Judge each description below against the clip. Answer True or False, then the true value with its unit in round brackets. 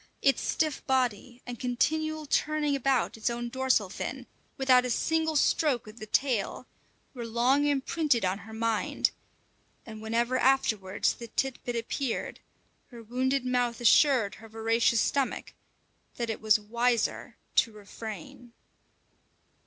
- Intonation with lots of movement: False (3.1 semitones)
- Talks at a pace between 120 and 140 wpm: True (135 wpm)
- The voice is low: False (245 Hz)